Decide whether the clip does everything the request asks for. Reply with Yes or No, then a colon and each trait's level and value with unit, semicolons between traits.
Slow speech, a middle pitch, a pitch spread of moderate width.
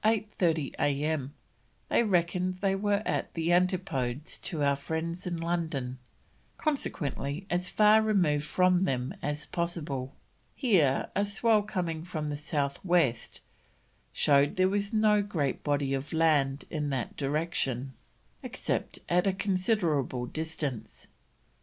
Yes: slow, 130 wpm; medium, 165 Hz; average, 4.6 semitones